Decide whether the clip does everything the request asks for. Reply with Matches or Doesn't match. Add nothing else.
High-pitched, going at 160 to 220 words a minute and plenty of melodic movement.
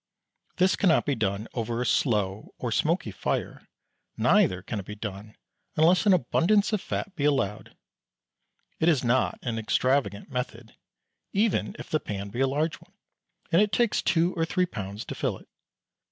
Doesn't match